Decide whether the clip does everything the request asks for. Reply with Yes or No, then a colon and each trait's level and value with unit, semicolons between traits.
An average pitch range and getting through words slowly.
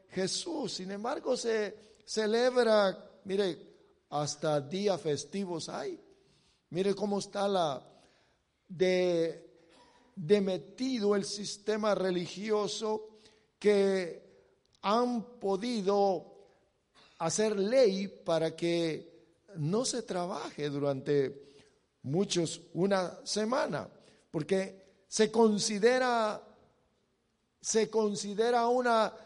Yes: average, 3.8 semitones; slow, 80 wpm